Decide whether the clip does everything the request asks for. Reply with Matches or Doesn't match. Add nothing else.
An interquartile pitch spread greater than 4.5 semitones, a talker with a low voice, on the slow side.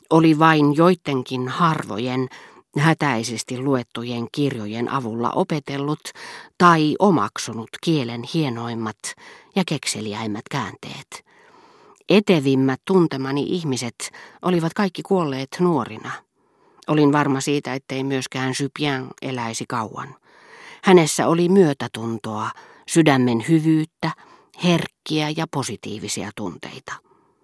Doesn't match